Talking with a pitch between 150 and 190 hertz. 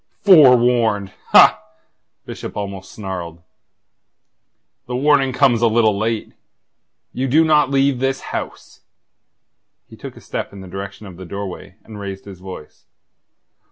No: low, 110 Hz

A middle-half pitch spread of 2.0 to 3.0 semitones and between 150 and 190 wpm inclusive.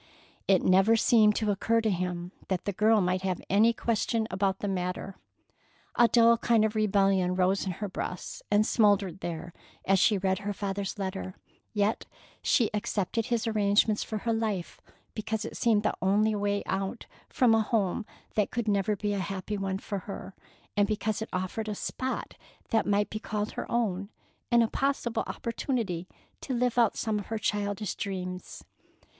Yes: narrow, 2.5 semitones; average, 175 wpm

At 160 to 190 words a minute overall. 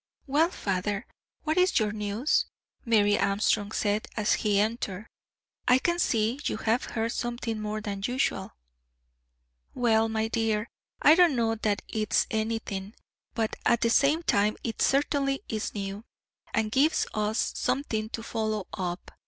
No: average, 145 wpm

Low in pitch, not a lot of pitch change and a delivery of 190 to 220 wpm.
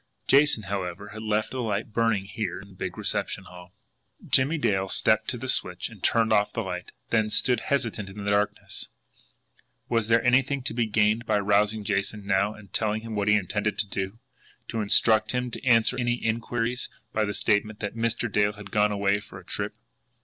Yes: low, 105 Hz; narrow, 2.2 semitones; average, 200 wpm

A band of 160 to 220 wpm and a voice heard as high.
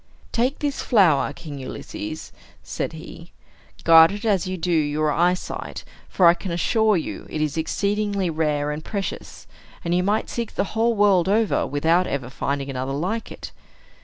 No: average, 165 wpm; medium, 175 Hz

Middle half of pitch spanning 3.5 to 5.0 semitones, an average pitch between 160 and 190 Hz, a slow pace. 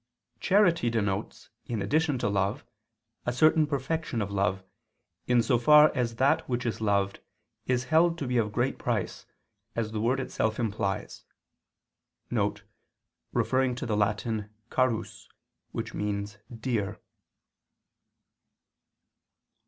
No: average, 4.1 semitones; low, 120 Hz; slow, 115 wpm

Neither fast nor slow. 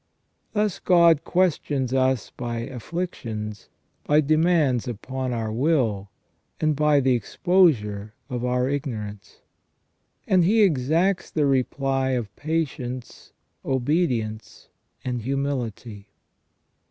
No: slow, 105 wpm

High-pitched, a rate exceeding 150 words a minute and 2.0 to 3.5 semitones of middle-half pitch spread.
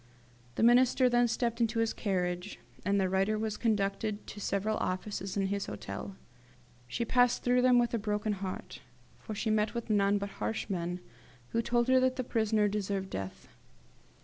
Yes: high, 210 Hz; average, 175 wpm; average, 3.2 semitones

